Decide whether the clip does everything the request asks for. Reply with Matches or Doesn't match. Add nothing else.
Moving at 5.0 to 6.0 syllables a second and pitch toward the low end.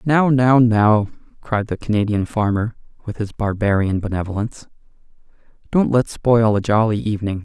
Matches